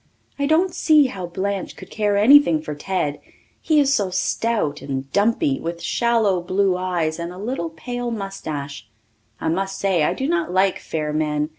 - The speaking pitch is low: No, high, 190 Hz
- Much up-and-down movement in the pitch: Yes, wide, 6.4 semitones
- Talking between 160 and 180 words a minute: Yes, average, 175 wpm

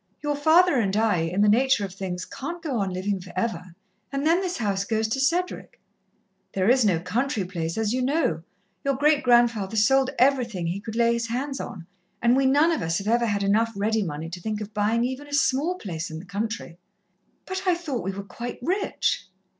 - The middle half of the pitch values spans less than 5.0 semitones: No, wide, 5.6 semitones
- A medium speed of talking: No, fast, 215 wpm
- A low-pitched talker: No, high, 225 Hz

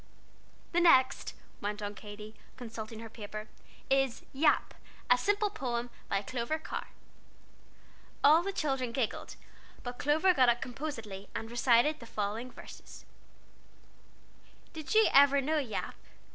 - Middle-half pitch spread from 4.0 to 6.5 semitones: Yes, average, 4.9 semitones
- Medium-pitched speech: No, very high, 250 Hz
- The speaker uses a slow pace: Yes, slow, 130 wpm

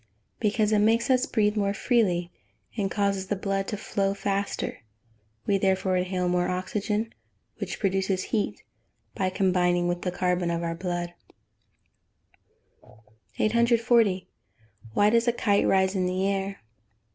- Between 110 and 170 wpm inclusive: Yes, average, 140 wpm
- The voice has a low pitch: No, high, 195 Hz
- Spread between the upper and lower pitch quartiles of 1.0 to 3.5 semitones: Yes, narrow, 2.4 semitones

